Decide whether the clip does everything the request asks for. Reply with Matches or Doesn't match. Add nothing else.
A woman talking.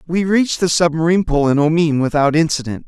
Doesn't match